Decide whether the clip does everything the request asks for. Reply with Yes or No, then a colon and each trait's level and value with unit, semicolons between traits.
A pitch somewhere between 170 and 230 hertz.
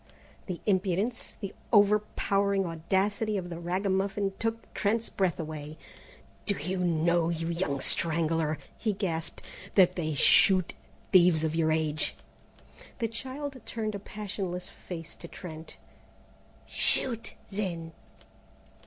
Yes: medium, 185 Hz